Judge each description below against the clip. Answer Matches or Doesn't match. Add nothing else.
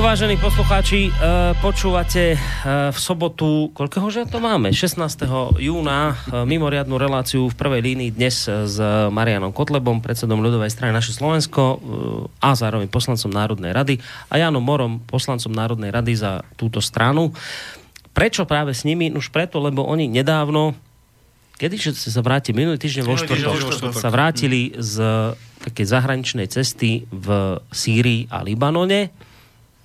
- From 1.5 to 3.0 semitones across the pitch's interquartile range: Doesn't match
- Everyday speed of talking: Matches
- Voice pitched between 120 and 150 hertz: Matches